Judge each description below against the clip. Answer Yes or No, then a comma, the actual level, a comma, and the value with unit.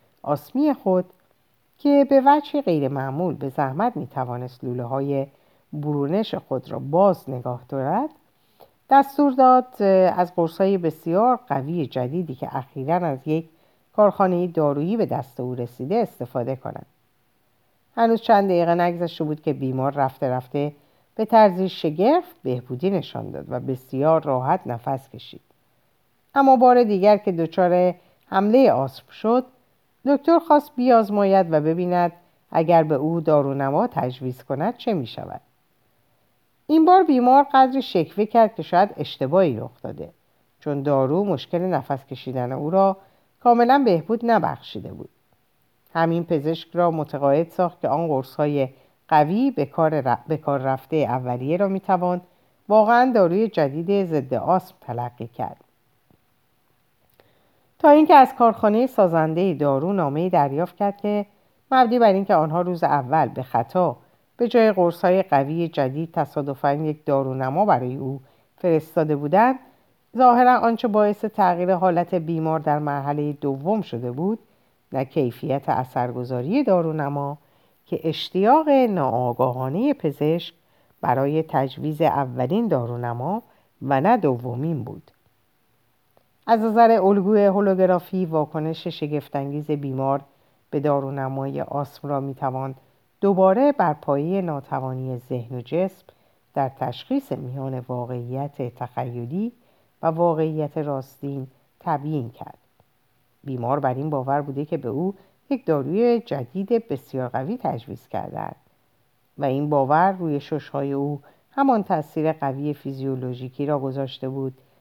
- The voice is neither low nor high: Yes, medium, 155 Hz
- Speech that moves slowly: No, average, 125 wpm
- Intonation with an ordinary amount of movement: No, wide, 6.2 semitones